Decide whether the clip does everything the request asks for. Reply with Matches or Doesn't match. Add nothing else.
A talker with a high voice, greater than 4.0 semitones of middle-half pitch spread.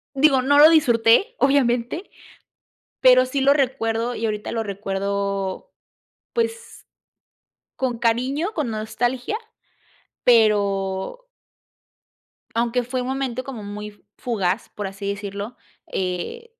Matches